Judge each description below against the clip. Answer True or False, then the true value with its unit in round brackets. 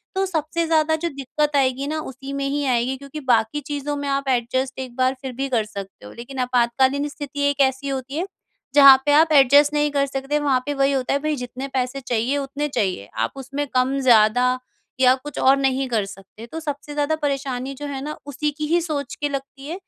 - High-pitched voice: True (275 Hz)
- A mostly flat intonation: True (2.3 semitones)